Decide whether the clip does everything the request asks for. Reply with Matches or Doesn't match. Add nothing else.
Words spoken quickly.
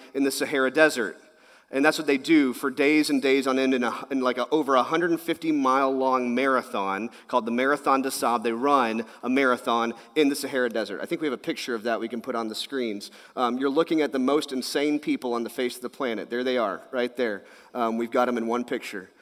Matches